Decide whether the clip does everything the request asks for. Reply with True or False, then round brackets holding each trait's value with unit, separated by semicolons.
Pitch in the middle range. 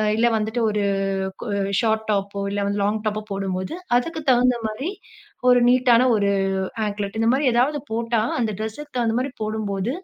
False (220 Hz)